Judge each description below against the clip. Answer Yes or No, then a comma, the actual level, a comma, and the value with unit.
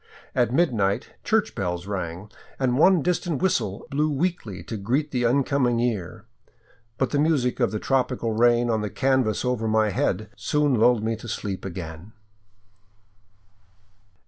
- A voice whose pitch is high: No, low, 120 Hz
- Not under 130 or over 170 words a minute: Yes, average, 145 wpm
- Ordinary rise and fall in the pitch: Yes, average, 4.4 semitones